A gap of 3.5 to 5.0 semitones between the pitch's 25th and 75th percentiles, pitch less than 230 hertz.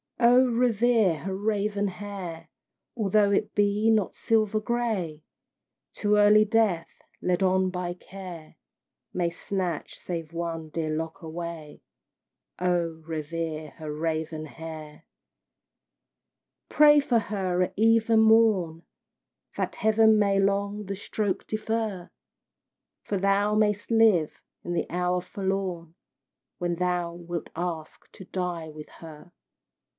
Yes: average, 4.0 semitones; medium, 185 Hz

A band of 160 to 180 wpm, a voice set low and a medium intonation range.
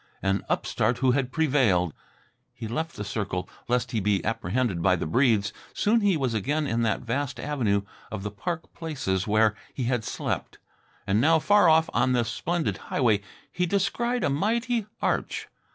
No: average, 170 wpm; low, 125 Hz; wide, 7.3 semitones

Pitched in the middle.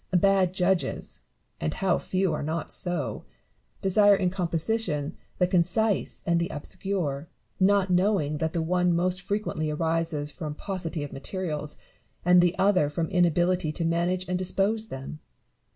Yes: medium, 175 Hz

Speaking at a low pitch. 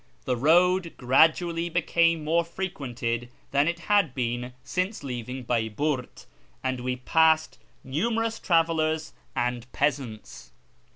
No: medium, 150 Hz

